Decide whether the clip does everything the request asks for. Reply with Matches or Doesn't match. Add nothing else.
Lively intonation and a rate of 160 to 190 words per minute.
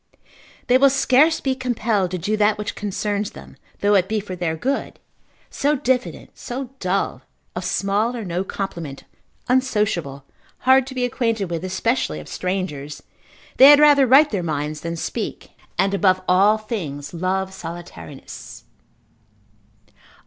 Doesn't match